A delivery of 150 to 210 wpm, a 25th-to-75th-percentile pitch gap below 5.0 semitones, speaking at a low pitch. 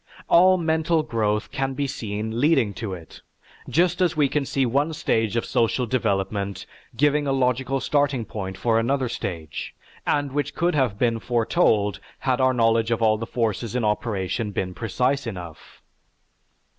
Yes: average, 160 wpm; average, 4.5 semitones; low, 120 Hz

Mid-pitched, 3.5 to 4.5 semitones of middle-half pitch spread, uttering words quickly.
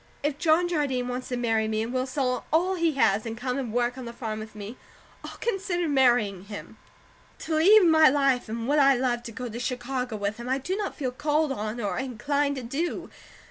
No: very high, 255 Hz; average, 4.0 semitones; fast, 220 wpm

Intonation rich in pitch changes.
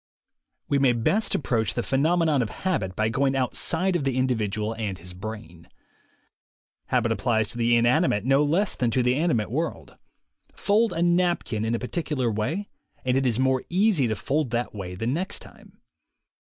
Yes: wide, 6.0 semitones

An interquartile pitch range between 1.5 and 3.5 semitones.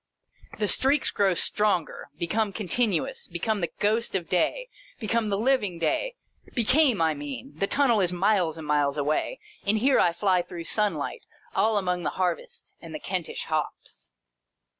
No: average, 5.0 semitones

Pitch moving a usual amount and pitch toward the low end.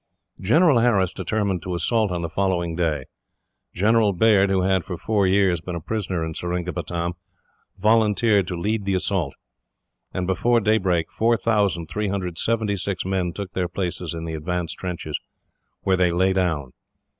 Yes: average, 3.0 semitones; very low, 95 Hz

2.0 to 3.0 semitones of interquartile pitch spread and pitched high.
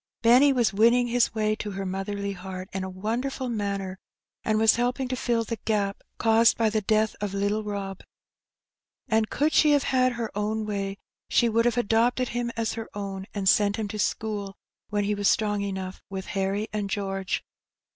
Yes: narrow, 2.6 semitones; high, 215 Hz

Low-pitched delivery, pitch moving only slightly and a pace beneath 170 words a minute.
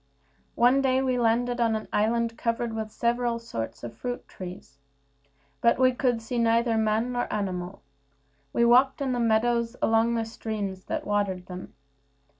No: high, 230 Hz; narrow, 2.3 semitones; average, 160 wpm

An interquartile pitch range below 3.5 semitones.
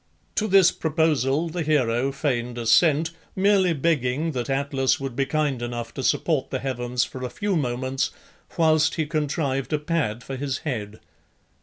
No: average, 4.0 semitones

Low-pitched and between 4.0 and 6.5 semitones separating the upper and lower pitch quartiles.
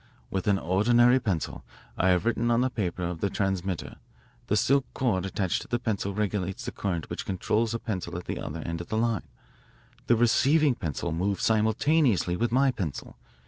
Yes: low, 100 Hz; average, 4.6 semitones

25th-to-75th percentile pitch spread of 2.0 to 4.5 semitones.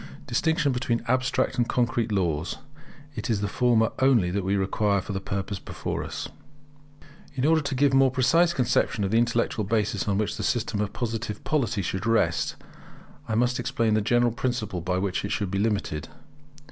Yes: average, 3.7 semitones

